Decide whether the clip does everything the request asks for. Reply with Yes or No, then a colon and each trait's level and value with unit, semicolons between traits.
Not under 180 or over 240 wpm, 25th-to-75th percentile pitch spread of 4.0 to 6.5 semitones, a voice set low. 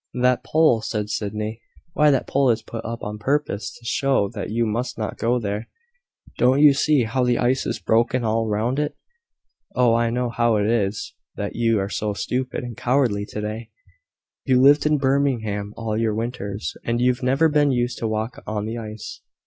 No: average, 195 wpm; average, 2.9 semitones; low, 115 Hz